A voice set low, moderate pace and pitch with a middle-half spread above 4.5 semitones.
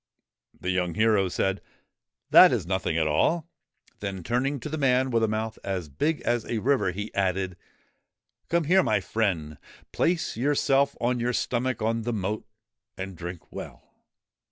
Yes: low, 110 Hz; average, 175 wpm; wide, 5.5 semitones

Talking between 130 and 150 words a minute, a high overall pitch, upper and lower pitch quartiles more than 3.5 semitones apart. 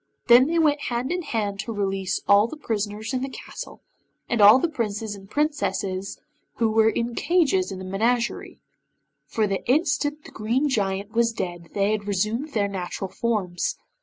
No: average, 175 wpm; high, 220 Hz; average, 4.6 semitones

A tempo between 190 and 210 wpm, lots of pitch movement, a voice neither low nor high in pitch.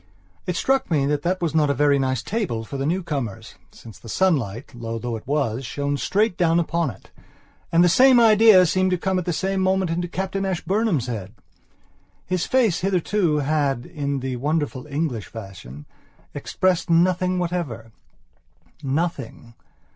No: average, 160 wpm; wide, 6.0 semitones; medium, 160 Hz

